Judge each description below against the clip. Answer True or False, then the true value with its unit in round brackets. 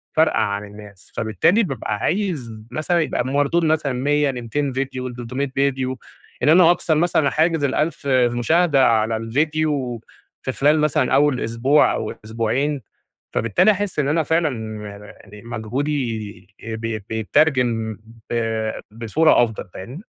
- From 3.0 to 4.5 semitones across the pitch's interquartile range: False (5.1 semitones)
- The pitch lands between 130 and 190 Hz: True (135 Hz)